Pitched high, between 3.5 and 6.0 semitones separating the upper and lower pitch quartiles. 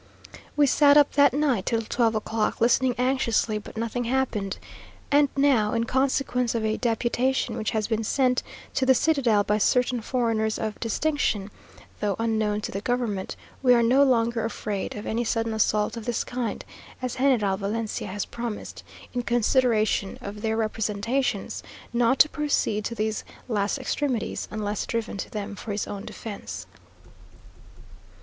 No: high, 230 Hz; average, 2.9 semitones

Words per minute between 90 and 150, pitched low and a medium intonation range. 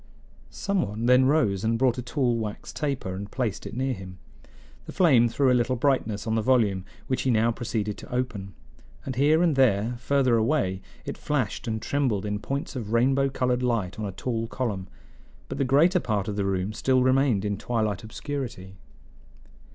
No: average, 190 wpm; low, 120 Hz; average, 4.2 semitones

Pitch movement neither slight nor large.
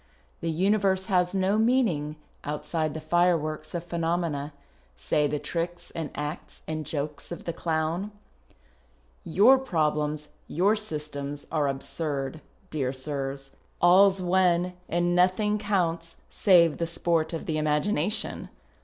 Yes: average, 3.4 semitones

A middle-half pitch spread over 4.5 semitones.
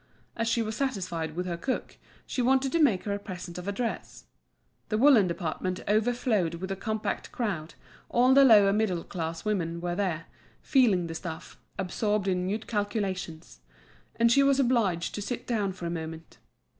Yes: average, 4.9 semitones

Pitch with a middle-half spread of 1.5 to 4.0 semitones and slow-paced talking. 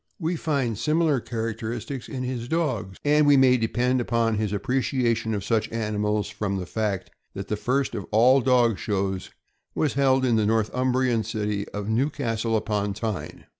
No: average, 3.5 semitones; average, 170 wpm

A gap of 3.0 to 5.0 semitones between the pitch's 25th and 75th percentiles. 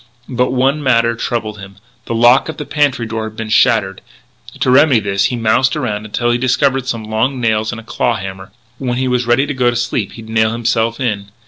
No: narrow, 2.6 semitones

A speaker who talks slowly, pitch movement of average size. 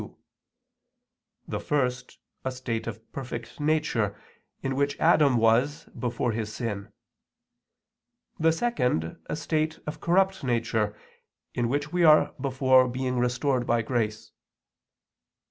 Yes: slow, 120 wpm; average, 4.2 semitones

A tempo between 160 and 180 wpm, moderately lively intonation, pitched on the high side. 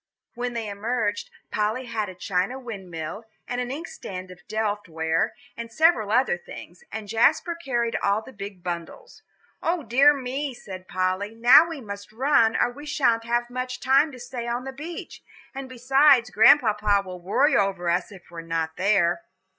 Yes: average, 170 wpm; average, 4.9 semitones; high, 225 Hz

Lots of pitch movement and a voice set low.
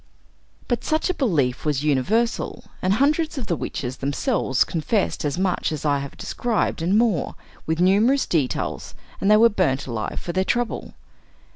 No: wide, 8.5 semitones; medium, 180 Hz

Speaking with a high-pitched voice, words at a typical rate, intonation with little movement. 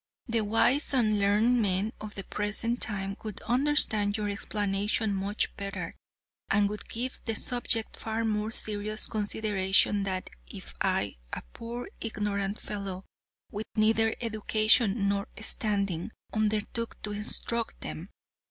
No: high, 210 Hz; slow, 130 wpm; narrow, 1.9 semitones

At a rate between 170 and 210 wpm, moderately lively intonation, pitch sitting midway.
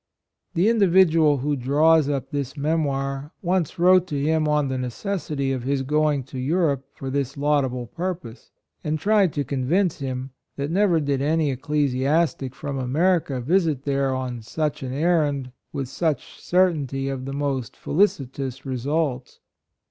No: average, 155 wpm; average, 3.3 semitones; medium, 145 Hz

